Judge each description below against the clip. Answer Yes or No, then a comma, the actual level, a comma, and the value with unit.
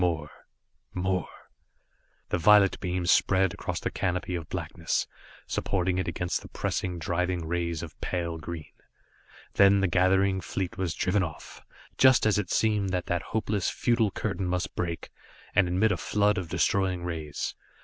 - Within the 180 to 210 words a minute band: No, average, 155 wpm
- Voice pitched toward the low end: Yes, very low, 90 Hz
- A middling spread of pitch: No, narrow, 2.1 semitones